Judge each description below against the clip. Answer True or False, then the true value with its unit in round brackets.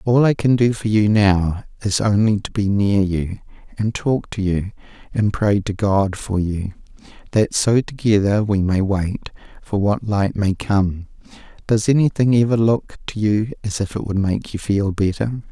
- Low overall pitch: True (105 Hz)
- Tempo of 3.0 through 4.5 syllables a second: True (4.4 syllables/s)